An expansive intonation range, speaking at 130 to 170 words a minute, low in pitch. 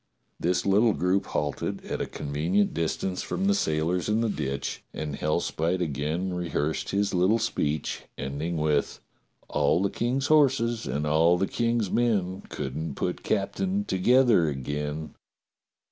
Yes: wide, 6.2 semitones; average, 150 wpm; very low, 90 Hz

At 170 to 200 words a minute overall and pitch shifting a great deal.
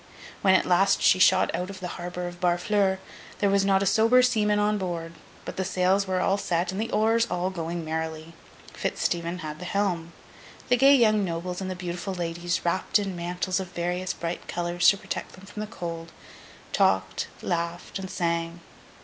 No: average, 190 wpm; narrow, 2.4 semitones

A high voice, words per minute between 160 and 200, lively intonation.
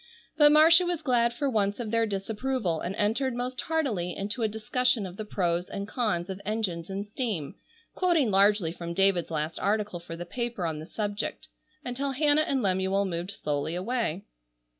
Yes: high, 210 Hz; average, 180 wpm; wide, 5.7 semitones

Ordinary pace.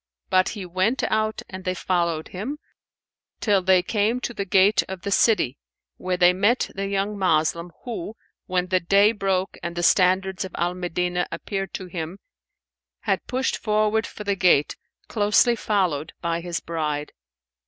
Yes: average, 165 wpm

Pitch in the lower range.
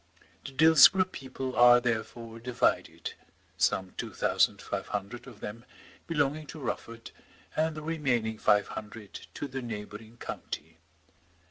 Yes: low, 120 Hz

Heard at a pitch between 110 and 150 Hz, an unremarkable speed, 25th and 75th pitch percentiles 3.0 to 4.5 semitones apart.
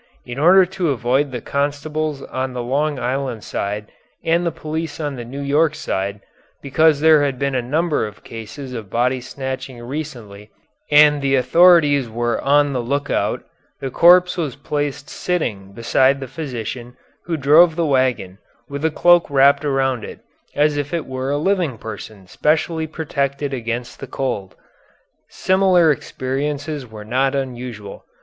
Yes: medium, 140 Hz; average, 155 wpm; average, 3.7 semitones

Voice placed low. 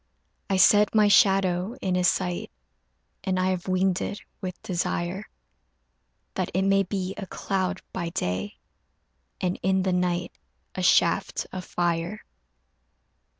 No: medium, 185 Hz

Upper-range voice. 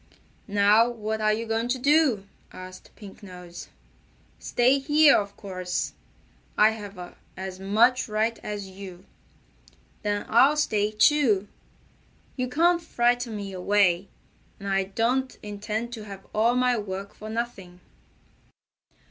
Yes: high, 215 Hz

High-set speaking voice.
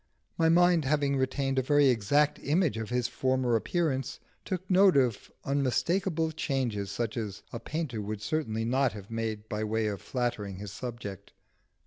No: low, 130 Hz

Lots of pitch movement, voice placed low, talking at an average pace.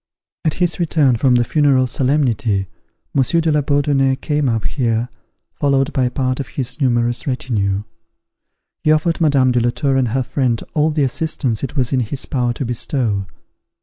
No: average, 3.3 semitones; low, 130 Hz; average, 175 wpm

